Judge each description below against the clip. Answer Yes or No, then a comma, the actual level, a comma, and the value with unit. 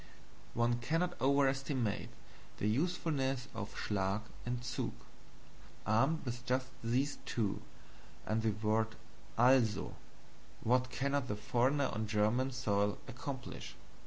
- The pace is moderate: No, slow, 110 wpm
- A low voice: Yes, low, 125 Hz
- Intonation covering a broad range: No, average, 3.6 semitones